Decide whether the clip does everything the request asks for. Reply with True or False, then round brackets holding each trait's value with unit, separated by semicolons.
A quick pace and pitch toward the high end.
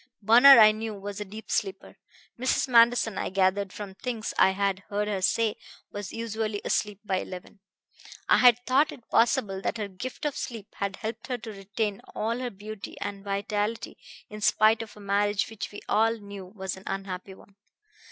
False (190 wpm; 210 Hz)